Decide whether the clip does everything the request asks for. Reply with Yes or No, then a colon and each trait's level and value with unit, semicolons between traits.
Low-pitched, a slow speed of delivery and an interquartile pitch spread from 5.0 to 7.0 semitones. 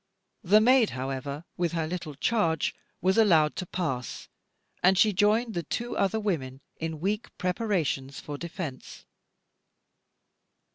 No: medium, 175 Hz; slow, 130 wpm; wide, 5.6 semitones